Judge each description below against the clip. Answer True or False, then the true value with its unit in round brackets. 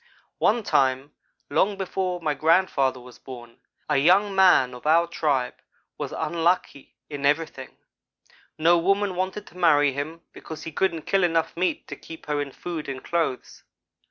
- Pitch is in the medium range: True (165 Hz)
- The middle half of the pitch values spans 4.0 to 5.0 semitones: True (4.4 semitones)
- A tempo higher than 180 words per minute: False (155 wpm)